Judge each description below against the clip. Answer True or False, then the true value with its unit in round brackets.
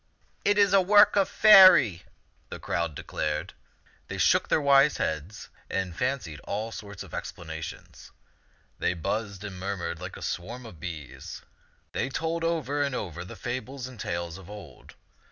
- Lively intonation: True (8.3 semitones)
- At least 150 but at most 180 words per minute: True (165 wpm)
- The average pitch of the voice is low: True (105 Hz)